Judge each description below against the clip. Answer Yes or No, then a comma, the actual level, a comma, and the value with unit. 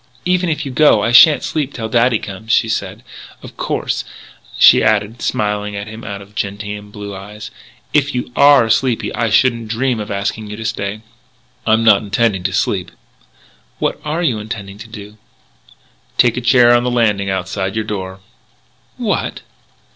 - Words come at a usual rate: Yes, average, 170 wpm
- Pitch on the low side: Yes, low, 110 Hz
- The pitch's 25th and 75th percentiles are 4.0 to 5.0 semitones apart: No, average, 2.9 semitones